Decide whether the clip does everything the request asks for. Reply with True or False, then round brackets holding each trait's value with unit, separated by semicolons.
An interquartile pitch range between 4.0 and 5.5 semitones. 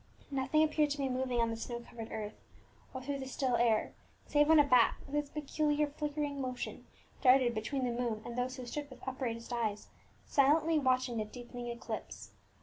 False (3.3 semitones)